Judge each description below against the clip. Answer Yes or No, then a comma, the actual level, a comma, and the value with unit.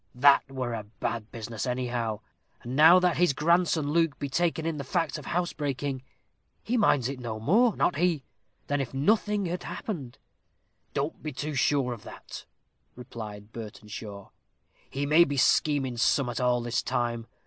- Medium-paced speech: Yes, average, 160 wpm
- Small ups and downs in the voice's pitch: No, average, 5.2 semitones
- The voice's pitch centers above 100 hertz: Yes, medium, 140 Hz